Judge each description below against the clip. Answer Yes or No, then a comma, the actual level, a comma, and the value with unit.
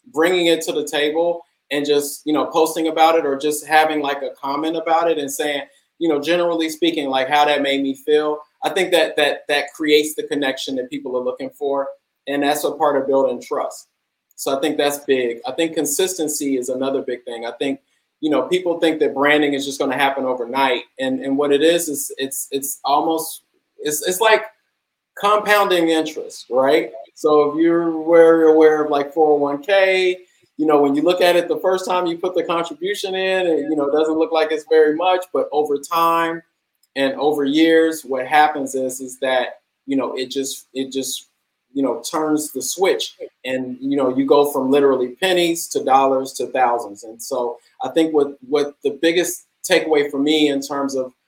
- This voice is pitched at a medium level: Yes, medium, 150 Hz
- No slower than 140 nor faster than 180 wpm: No, average, 200 wpm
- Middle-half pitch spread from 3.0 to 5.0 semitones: Yes, average, 3.3 semitones